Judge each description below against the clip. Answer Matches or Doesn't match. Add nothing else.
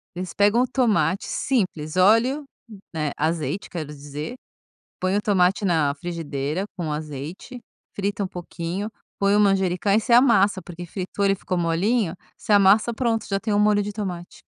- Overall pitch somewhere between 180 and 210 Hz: Matches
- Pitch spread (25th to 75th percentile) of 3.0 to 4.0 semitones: Matches